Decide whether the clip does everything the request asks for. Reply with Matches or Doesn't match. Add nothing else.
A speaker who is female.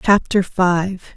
Matches